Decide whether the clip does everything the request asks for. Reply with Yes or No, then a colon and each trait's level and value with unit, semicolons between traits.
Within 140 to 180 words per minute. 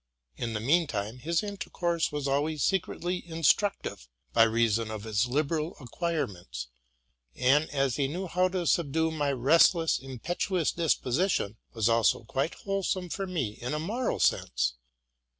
Yes: average, 145 wpm